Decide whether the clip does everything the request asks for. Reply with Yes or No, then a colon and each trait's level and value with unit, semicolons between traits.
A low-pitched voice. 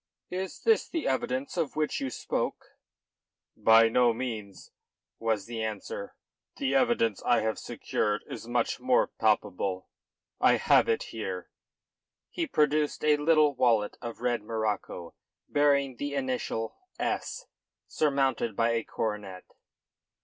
Yes: low, 125 Hz